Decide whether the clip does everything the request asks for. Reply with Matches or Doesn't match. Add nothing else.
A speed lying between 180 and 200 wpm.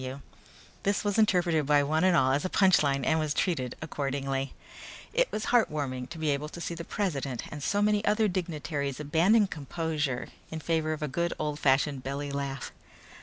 Matches